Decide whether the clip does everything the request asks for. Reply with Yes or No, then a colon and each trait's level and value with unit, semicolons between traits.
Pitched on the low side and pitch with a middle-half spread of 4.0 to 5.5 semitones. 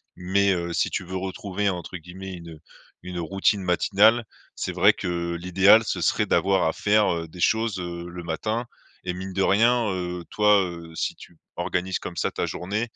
No: very low, 95 Hz; narrow, 2.6 semitones